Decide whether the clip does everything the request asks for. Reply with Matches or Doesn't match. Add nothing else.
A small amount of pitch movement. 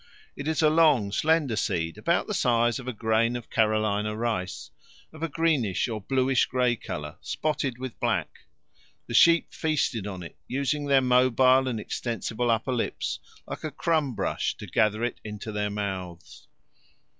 Doesn't match